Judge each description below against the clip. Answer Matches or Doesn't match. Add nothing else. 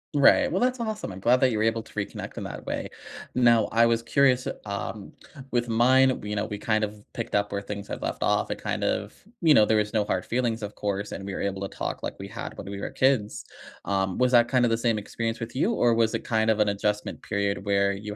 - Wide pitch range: Doesn't match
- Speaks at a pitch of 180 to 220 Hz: Doesn't match